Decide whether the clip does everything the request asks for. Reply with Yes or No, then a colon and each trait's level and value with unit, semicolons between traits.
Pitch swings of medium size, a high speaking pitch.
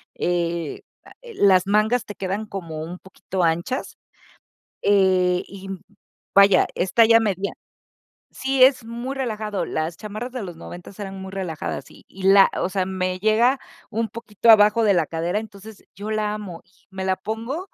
Yes: average, 3.1 semitones; high, 200 Hz